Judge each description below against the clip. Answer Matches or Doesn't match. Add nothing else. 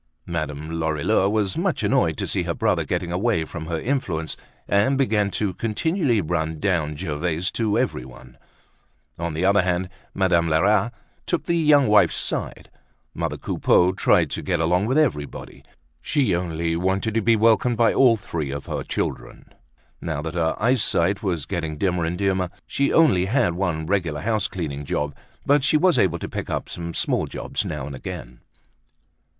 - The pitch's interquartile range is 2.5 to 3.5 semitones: Doesn't match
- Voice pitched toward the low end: Matches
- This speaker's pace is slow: Doesn't match